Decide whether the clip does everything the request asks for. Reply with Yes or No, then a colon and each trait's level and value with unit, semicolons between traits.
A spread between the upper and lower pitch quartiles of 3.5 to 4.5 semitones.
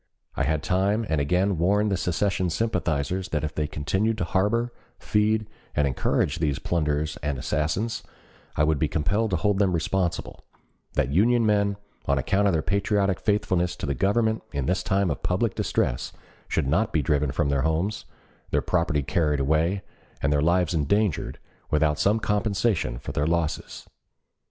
No: average, 5.2 semitones